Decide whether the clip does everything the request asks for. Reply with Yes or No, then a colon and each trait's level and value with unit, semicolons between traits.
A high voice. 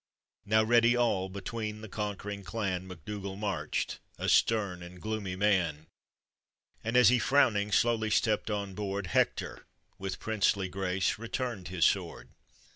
No: low, 100 Hz